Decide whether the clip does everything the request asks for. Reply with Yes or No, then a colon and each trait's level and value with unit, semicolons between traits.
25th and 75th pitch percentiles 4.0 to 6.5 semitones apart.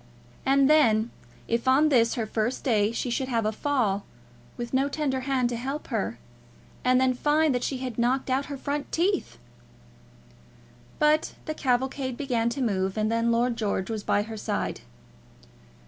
No: average, 3.2 semitones